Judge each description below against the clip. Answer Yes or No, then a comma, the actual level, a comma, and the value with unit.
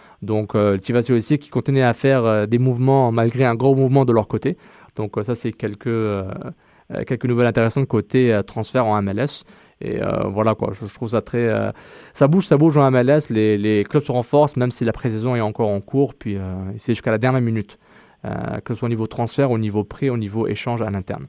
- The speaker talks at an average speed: No, fast, 235 wpm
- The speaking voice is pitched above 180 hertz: No, low, 120 Hz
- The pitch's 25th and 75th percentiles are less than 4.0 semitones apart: Yes, average, 3.4 semitones